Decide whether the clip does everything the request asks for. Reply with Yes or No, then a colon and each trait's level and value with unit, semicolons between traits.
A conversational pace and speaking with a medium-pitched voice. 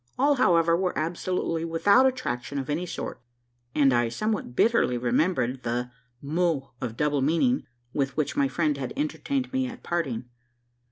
Yes: average, 155 wpm; medium, 160 Hz